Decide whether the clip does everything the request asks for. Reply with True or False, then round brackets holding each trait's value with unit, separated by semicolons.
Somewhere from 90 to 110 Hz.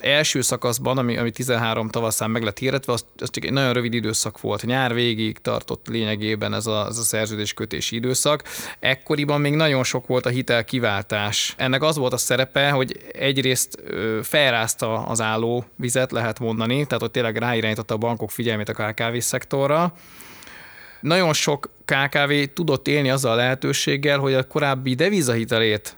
False (125 Hz)